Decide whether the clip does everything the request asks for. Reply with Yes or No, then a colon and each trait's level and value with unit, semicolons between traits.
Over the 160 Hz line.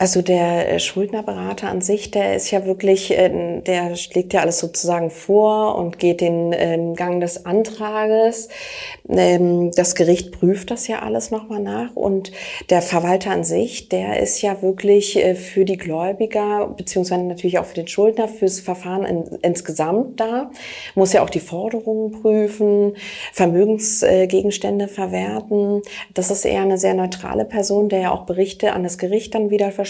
Yes: high, 190 Hz